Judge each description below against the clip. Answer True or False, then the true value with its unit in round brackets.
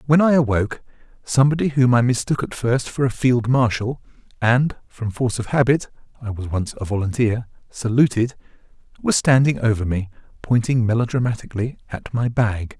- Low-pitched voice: True (120 Hz)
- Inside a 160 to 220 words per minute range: False (145 wpm)